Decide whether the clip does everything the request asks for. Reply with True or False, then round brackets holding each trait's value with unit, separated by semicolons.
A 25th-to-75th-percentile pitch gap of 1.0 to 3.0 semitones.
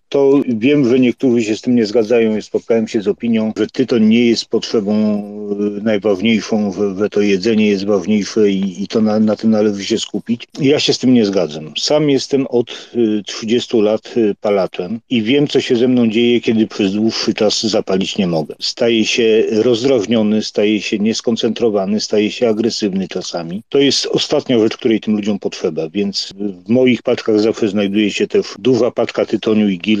True (2.4 semitones)